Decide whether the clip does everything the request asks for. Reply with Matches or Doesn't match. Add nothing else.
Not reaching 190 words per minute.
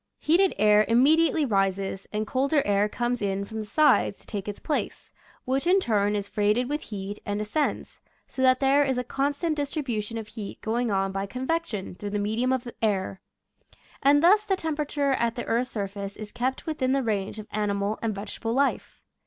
Doesn't match